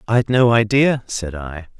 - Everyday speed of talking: Yes, average, 165 wpm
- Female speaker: No, male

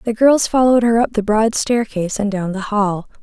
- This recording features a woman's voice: Yes, female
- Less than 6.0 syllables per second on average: Yes, 5.3 syllables/s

